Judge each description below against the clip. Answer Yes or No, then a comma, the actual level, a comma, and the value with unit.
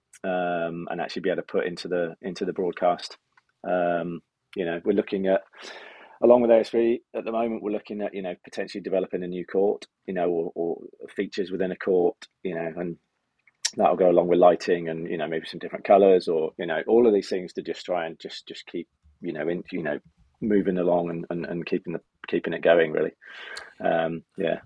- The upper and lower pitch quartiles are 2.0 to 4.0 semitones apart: Yes, average, 3.3 semitones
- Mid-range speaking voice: No, very low, 90 Hz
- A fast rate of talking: Yes, fast, 215 wpm